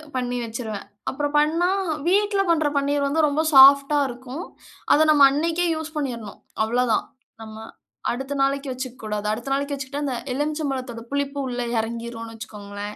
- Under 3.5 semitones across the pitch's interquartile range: No, average, 3.8 semitones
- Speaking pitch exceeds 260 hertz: Yes, very high, 270 Hz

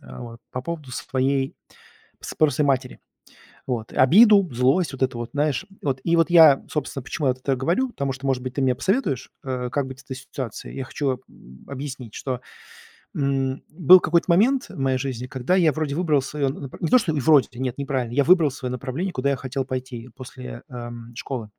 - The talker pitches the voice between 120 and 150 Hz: Yes, low, 135 Hz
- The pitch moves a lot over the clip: No, average, 3.1 semitones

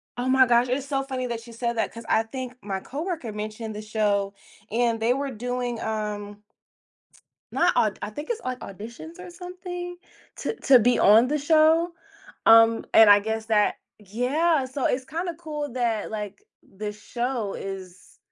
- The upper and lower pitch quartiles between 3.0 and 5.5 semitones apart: Yes, average, 4.4 semitones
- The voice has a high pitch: Yes, high, 240 Hz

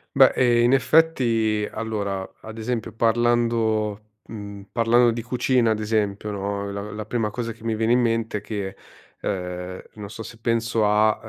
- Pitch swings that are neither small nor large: No, narrow, 2.1 semitones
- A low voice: Yes, low, 110 Hz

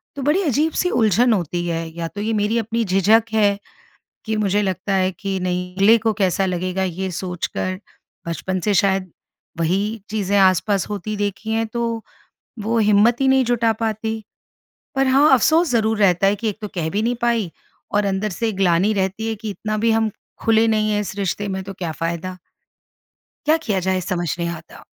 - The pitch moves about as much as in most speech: Yes, average, 3.2 semitones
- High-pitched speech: Yes, high, 205 Hz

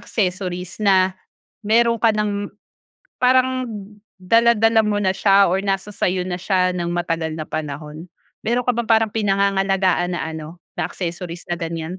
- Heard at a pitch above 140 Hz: Yes, high, 190 Hz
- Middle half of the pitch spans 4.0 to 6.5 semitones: No, average, 3.5 semitones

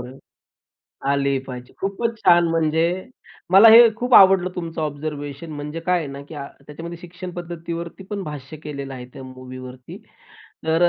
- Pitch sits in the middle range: Yes, medium, 160 Hz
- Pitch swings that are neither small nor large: Yes, average, 4.1 semitones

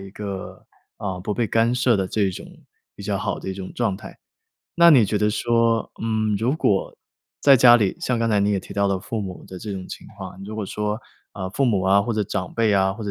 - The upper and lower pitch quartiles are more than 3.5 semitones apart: No, average, 2.8 semitones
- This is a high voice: No, low, 105 Hz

